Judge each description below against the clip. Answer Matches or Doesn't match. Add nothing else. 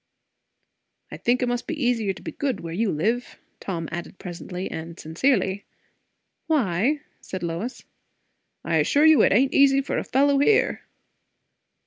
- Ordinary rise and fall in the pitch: Doesn't match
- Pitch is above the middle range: Matches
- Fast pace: Doesn't match